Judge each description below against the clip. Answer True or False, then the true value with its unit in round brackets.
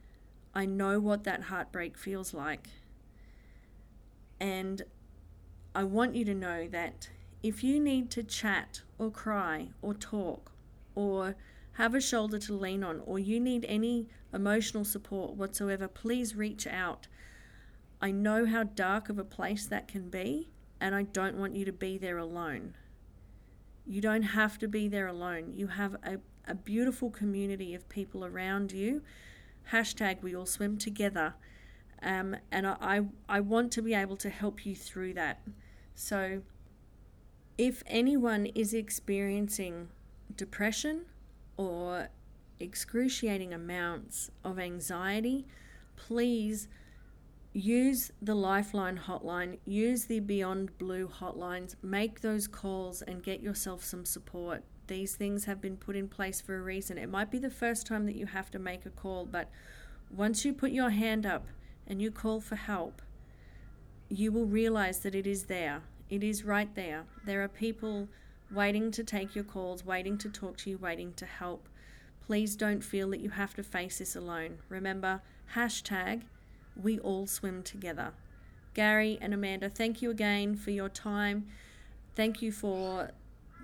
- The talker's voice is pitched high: True (200 Hz)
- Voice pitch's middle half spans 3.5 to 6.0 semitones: False (2.5 semitones)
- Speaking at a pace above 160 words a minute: False (155 wpm)